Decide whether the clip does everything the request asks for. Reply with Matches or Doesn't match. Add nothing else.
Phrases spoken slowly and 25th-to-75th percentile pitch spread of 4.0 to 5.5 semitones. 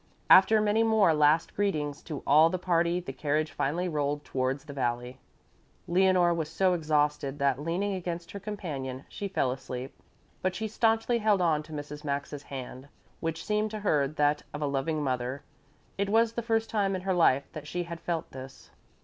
Doesn't match